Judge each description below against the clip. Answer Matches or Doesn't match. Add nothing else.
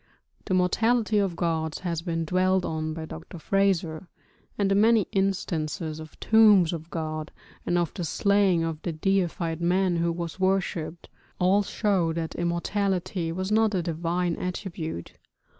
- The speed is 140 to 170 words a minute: Matches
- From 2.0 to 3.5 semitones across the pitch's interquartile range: Matches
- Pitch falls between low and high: Matches